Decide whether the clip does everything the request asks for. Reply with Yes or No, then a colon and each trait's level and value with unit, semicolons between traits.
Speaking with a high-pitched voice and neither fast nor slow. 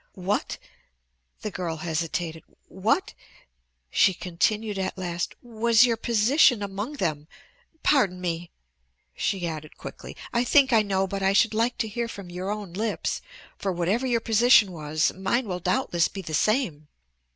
Yes: high, 195 Hz; average, 150 wpm